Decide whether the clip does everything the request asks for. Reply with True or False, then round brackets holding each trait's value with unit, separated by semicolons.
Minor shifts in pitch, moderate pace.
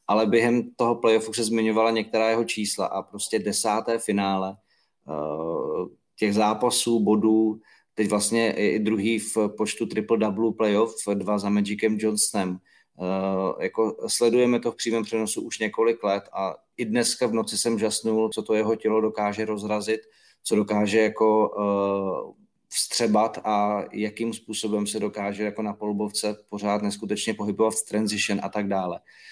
True (1.4 semitones; 145 wpm)